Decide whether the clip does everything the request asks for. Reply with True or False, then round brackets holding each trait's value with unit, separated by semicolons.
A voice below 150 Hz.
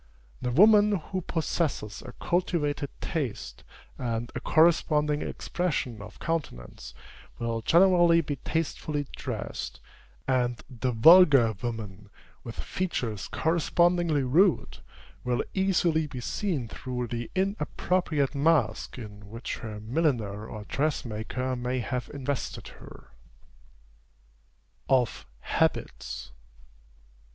True (135 Hz)